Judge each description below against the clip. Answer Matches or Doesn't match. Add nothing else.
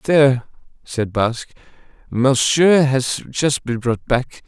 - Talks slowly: Matches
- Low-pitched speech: Matches